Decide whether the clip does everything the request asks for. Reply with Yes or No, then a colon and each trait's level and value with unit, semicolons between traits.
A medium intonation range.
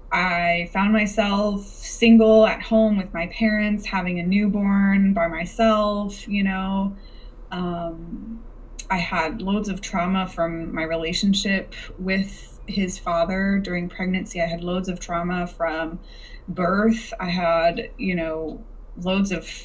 Yes: average, 3.0 semitones